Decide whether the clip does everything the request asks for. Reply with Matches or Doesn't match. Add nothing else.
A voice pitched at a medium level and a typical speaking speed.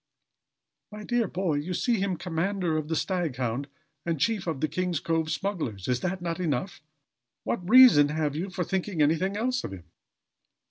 Matches